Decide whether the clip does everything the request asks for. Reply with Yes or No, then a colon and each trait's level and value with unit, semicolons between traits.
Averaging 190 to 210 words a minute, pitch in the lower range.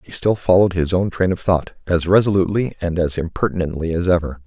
Yes: average, 200 wpm; very low, 90 Hz